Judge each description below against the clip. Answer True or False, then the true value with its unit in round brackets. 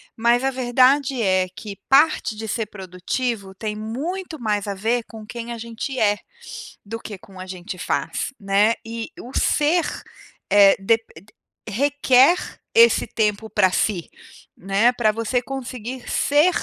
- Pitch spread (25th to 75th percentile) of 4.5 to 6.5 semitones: False (3.9 semitones)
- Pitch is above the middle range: True (225 Hz)